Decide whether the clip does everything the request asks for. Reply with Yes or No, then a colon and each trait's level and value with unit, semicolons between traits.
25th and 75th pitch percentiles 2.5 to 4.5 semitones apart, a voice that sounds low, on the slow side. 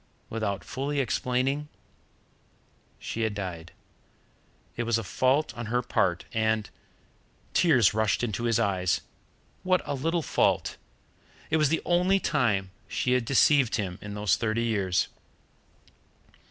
No: average, 5.0 semitones; low, 115 Hz; slow, 130 wpm